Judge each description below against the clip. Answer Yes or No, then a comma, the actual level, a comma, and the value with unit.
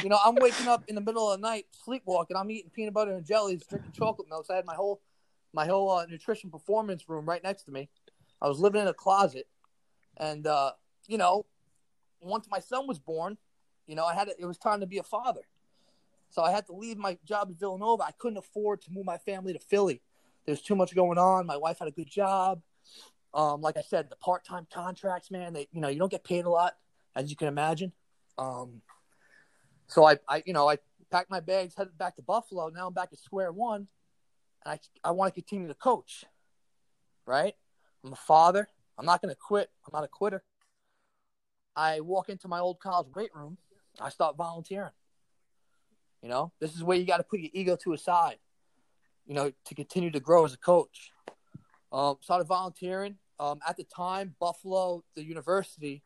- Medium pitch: Yes, medium, 180 Hz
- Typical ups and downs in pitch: Yes, average, 3.7 semitones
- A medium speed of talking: No, fast, 210 wpm